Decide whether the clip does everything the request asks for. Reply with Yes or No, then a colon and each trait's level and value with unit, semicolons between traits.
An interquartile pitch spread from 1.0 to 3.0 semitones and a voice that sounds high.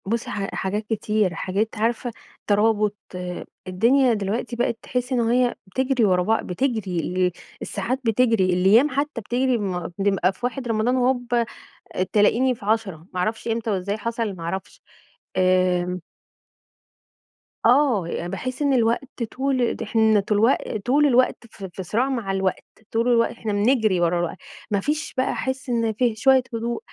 No: average, 4.2 semitones; high, 225 Hz